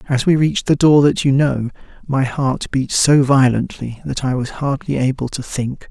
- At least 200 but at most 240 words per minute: Yes, fast, 205 wpm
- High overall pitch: No, low, 135 Hz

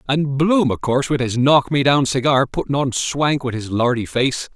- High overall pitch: No, low, 135 Hz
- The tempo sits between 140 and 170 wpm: No, average, 200 wpm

